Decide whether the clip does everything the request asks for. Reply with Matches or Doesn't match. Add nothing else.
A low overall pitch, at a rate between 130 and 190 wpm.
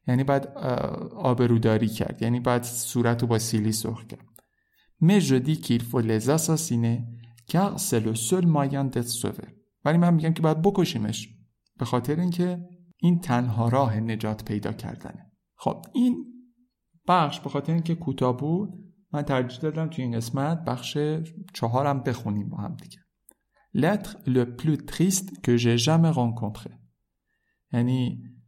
Matches